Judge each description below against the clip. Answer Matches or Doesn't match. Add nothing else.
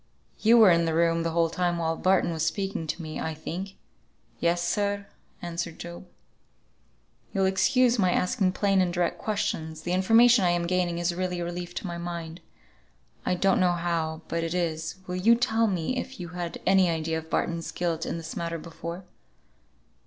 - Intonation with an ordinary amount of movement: Doesn't match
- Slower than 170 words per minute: Doesn't match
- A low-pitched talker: Doesn't match